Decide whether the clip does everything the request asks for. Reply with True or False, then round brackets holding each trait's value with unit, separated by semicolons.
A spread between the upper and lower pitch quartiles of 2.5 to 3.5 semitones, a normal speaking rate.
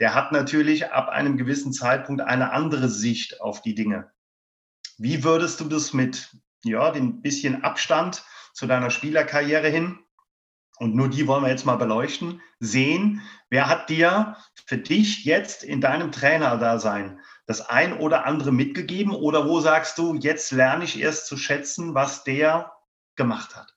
False (3.9 semitones; 160 wpm)